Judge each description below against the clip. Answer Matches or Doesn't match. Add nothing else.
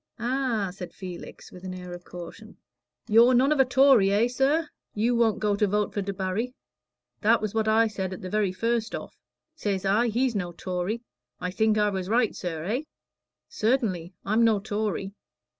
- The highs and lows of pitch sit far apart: Doesn't match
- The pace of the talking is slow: Doesn't match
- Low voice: Doesn't match